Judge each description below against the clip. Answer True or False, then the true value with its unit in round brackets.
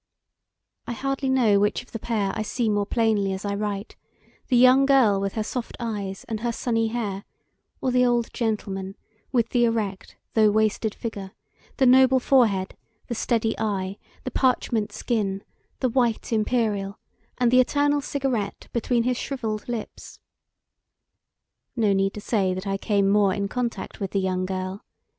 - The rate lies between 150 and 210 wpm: True (165 wpm)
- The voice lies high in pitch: True (220 Hz)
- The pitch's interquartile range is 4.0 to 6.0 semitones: False (3.5 semitones)